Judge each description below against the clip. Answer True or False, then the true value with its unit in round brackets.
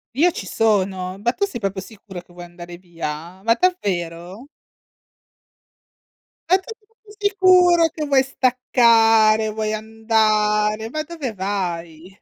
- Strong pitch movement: True (6.2 semitones)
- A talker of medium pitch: False (215 Hz)